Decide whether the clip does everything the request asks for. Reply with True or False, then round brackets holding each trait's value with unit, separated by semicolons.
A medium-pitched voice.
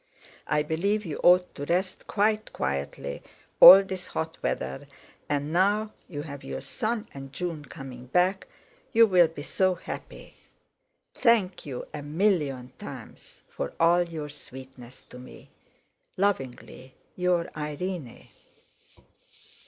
True (165 Hz)